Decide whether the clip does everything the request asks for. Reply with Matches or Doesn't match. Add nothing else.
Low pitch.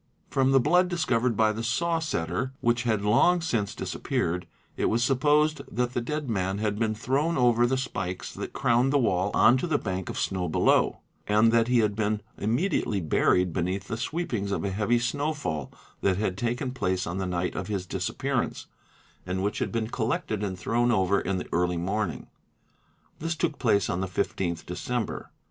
Matches